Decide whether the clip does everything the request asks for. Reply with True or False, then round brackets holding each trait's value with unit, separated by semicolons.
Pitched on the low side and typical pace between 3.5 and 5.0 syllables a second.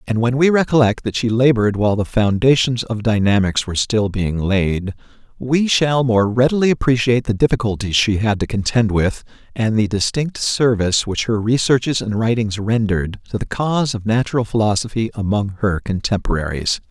False (110 Hz; 5.4 syllables/s)